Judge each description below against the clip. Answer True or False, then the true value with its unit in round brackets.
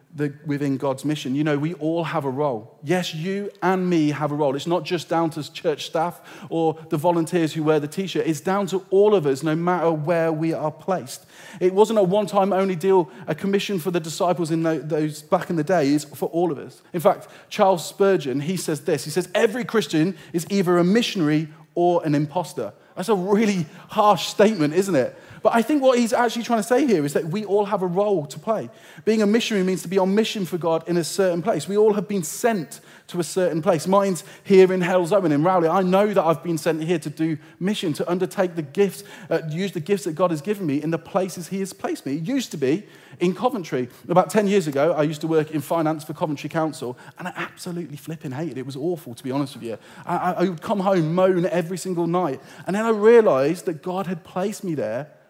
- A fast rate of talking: True (240 wpm)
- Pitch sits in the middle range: True (175 Hz)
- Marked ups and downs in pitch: False (3.6 semitones)